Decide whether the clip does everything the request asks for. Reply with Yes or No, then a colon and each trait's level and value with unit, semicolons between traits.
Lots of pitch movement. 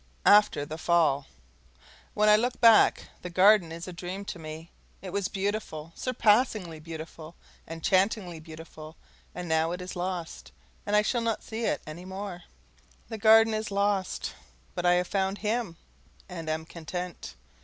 No: average, 4.2 semitones